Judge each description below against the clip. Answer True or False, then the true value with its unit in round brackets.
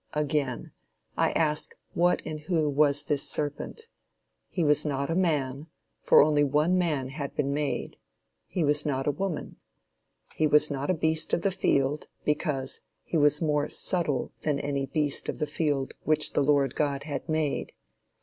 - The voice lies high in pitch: False (150 Hz)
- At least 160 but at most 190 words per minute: True (170 wpm)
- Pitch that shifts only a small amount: True (1.9 semitones)